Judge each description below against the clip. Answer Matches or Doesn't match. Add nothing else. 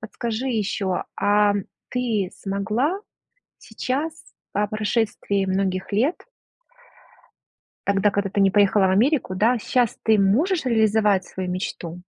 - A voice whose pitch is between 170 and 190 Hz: Doesn't match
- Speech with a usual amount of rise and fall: Matches